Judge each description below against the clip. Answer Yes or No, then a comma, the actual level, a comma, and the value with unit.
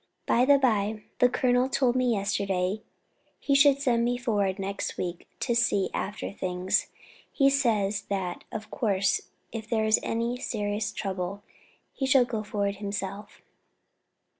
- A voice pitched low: No, high, 215 Hz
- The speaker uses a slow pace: No, average, 145 wpm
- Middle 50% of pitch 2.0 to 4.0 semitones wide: Yes, average, 3.7 semitones